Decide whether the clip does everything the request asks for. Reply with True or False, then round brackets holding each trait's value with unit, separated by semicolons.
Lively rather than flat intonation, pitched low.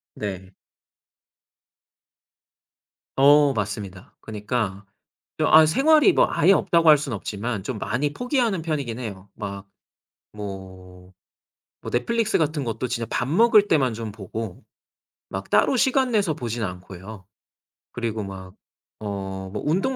True (7.9 semitones; 115 Hz)